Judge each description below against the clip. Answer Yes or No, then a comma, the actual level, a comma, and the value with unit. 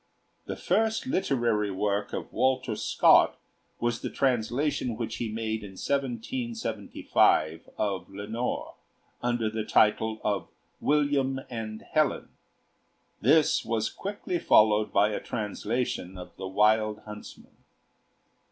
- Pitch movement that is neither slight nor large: Yes, average, 3.8 semitones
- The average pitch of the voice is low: Yes, low, 110 Hz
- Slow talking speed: Yes, slow, 115 wpm